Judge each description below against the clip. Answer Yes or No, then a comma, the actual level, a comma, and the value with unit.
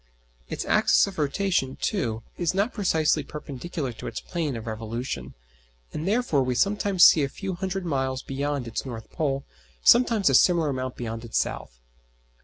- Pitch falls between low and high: Yes, medium, 145 Hz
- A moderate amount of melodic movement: No, wide, 6.5 semitones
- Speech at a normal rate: Yes, average, 165 wpm